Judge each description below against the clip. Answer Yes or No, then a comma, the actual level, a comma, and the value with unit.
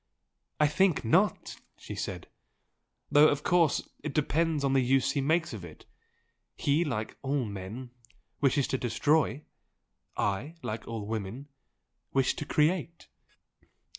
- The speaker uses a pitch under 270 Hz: Yes, medium, 140 Hz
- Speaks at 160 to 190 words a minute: No, slow, 135 wpm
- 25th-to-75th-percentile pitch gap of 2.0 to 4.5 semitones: No, average, 5.0 semitones